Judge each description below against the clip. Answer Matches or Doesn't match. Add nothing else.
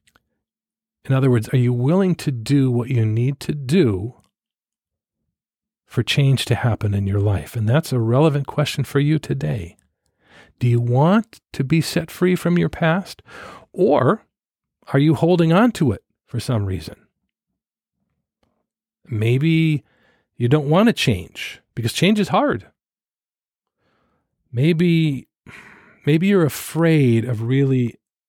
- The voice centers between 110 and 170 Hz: Matches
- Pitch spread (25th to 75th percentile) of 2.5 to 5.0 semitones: Doesn't match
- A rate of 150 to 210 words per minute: Doesn't match